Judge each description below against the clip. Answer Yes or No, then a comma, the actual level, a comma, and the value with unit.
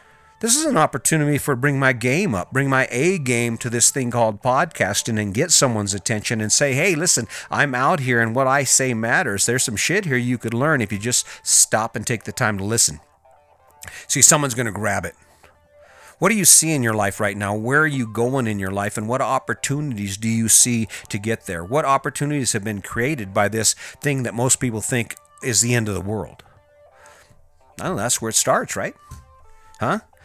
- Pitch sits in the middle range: No, low, 120 Hz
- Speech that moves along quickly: Yes, fast, 215 wpm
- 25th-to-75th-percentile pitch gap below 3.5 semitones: No, average, 4.1 semitones